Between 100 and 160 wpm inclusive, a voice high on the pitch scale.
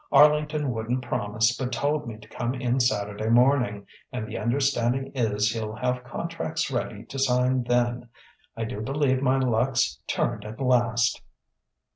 No: average, 150 wpm; low, 125 Hz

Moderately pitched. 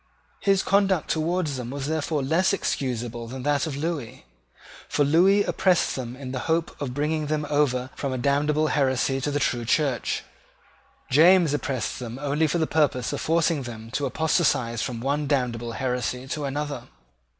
Yes: medium, 145 Hz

